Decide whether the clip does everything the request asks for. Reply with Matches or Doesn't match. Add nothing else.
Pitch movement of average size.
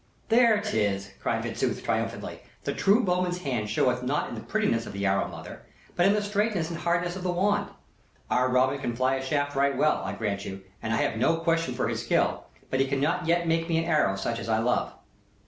Doesn't match